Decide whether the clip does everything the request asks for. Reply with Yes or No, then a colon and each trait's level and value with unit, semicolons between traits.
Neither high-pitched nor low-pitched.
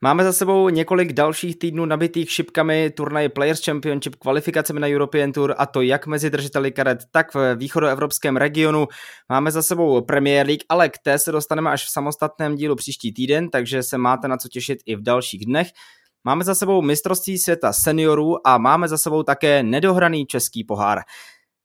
Yes: medium, 150 Hz